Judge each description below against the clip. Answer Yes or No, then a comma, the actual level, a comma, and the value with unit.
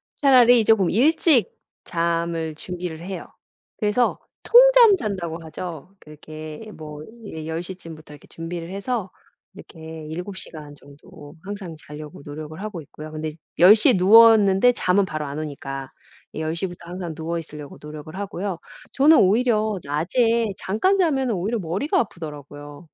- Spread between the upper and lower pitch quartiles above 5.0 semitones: Yes, wide, 5.4 semitones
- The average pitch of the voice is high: No, medium, 175 Hz